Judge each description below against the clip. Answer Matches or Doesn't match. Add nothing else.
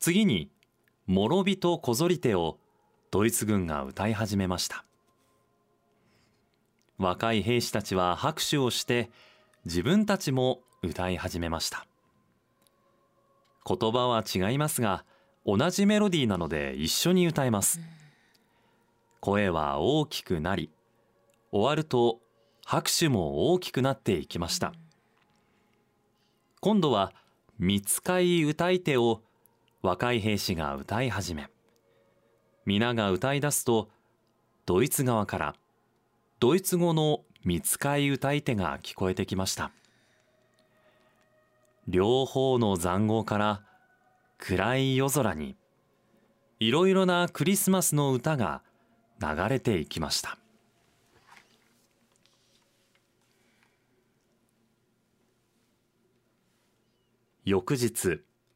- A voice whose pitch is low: Matches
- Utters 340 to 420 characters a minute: Doesn't match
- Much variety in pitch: Doesn't match